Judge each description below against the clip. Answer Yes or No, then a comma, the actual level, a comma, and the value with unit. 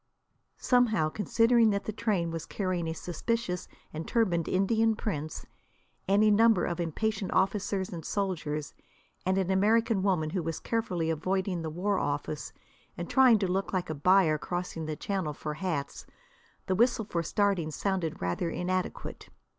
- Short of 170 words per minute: Yes, average, 155 wpm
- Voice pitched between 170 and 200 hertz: Yes, medium, 185 Hz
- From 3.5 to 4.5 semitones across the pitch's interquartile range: Yes, average, 4.2 semitones